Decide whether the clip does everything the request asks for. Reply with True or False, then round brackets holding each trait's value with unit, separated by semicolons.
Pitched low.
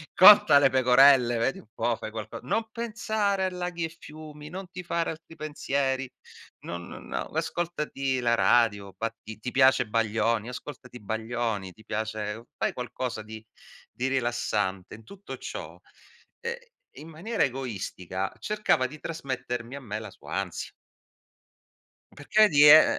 True (130 Hz)